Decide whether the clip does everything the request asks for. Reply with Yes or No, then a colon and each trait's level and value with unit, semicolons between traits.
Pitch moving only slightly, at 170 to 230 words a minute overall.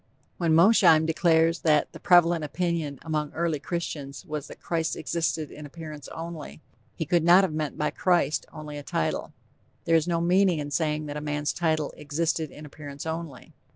Yes: narrow, 2.1 semitones; average, 180 wpm